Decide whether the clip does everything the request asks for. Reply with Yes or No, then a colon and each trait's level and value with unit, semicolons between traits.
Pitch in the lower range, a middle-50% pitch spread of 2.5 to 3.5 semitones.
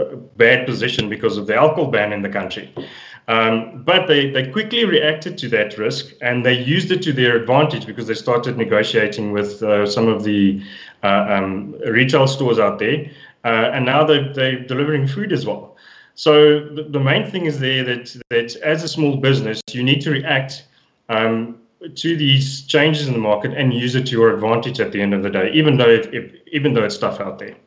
No: low, 125 Hz; average, 4.6 semitones